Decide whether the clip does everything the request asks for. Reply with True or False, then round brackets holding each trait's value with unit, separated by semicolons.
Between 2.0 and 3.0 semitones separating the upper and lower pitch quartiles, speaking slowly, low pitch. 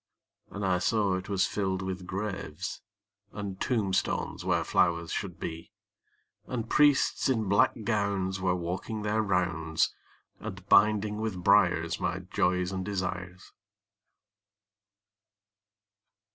True (2.4 semitones; 115 wpm; 95 Hz)